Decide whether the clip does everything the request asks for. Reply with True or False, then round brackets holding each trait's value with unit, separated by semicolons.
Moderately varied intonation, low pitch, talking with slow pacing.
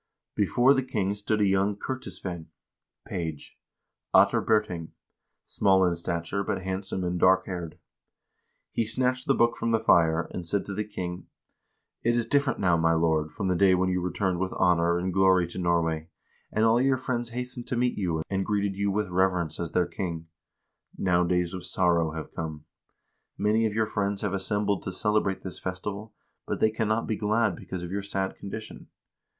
False (3.4 semitones; 95 Hz; 190 wpm)